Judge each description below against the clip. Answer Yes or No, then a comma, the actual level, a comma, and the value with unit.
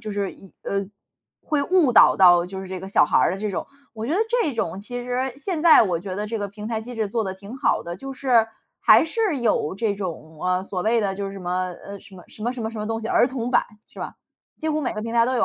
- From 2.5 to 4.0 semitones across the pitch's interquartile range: No, average, 4.4 semitones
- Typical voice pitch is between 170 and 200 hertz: No, high, 215 Hz